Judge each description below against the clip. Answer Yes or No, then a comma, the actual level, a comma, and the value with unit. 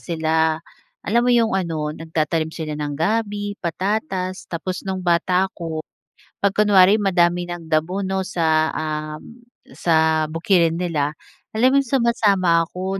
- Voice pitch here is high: No, medium, 175 Hz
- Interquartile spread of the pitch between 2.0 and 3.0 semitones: No, average, 3.8 semitones